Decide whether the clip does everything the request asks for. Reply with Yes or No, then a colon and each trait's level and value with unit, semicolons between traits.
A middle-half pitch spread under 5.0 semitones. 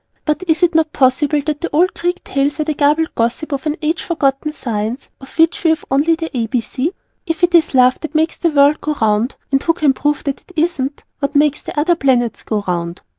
Yes: average, 3.4 semitones